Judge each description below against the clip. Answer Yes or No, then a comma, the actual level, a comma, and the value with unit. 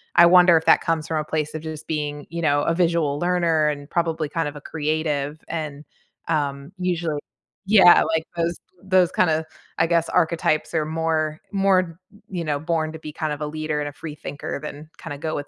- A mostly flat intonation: Yes, narrow, 1.9 semitones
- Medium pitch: Yes, medium, 160 Hz